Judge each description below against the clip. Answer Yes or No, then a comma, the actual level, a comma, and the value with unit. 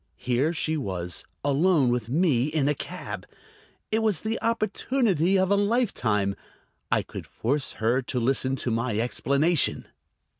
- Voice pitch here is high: No, medium, 145 Hz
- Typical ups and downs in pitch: No, wide, 7.6 semitones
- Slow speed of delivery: No, average, 145 wpm